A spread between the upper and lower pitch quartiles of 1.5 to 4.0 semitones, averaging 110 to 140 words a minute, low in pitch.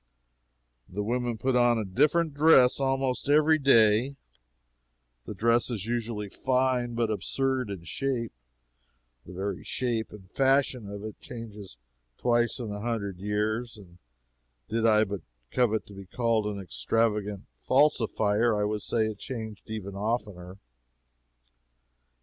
Yes: average, 3.3 semitones; slow, 135 wpm; low, 115 Hz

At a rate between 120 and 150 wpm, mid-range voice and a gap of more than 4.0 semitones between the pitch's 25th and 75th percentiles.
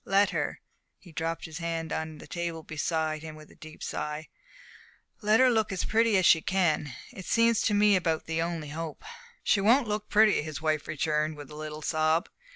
No: average, 200 wpm; medium, 165 Hz; average, 4.5 semitones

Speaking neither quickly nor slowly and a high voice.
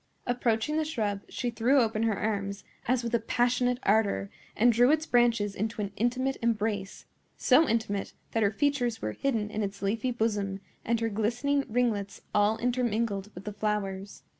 Yes: average, 165 wpm; high, 225 Hz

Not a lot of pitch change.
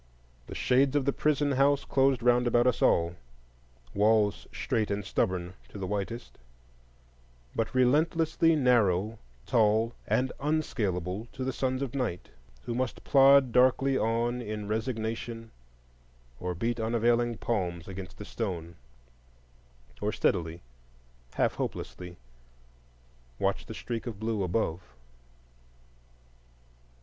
No: average, 4.2 semitones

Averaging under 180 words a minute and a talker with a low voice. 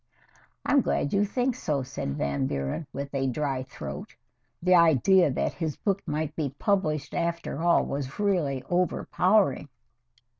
No: average, 150 wpm; medium, 155 Hz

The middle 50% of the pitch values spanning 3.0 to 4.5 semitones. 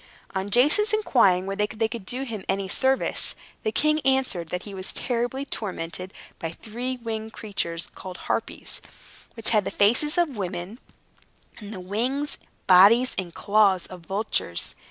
No: average, 5.0 semitones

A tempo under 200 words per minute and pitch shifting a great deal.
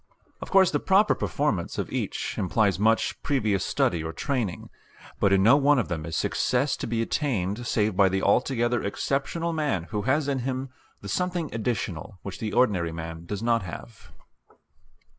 Yes: average, 175 wpm; wide, 6.1 semitones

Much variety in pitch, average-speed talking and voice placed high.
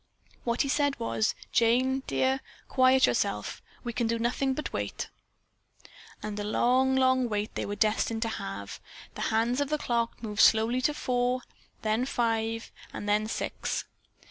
No: average, 2.8 semitones; average, 160 wpm; high, 235 Hz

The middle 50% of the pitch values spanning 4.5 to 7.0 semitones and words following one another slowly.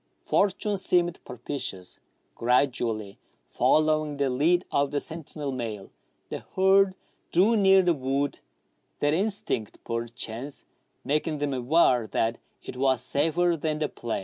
Yes: wide, 5.6 semitones; slow, 130 wpm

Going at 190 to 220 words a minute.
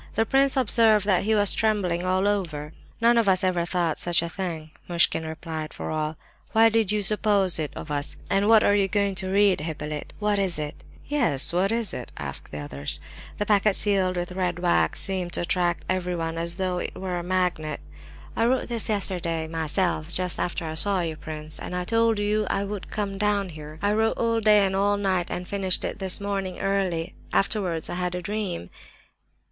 Yes: average, 200 wpm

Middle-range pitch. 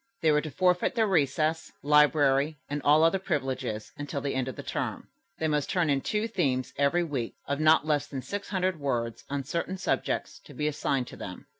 Yes: medium, 150 Hz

